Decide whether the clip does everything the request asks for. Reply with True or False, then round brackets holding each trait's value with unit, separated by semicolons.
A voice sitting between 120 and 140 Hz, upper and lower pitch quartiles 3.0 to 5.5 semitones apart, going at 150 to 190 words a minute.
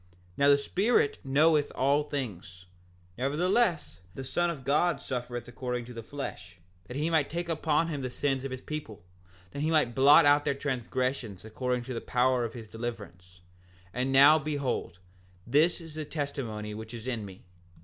True (135 Hz; 4.0 semitones; 180 wpm)